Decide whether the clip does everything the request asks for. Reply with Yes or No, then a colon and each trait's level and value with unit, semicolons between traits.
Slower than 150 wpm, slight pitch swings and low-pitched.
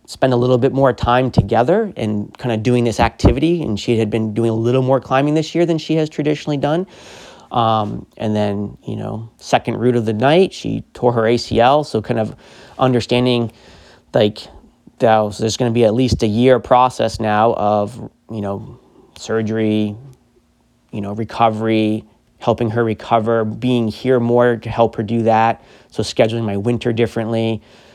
No: average, 175 wpm; narrow, 2.3 semitones; low, 115 Hz